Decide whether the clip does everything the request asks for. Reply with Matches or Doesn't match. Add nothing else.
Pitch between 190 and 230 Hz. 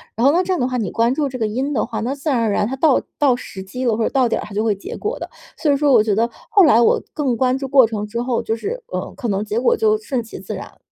Doesn't match